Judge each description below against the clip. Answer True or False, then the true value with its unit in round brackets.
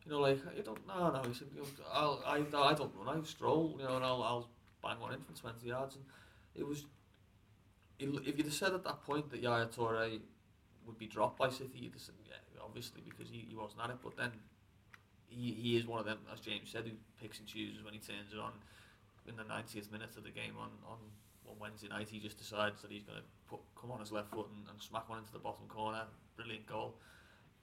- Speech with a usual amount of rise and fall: False (2.3 semitones)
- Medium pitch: False (110 Hz)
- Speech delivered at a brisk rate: True (240 wpm)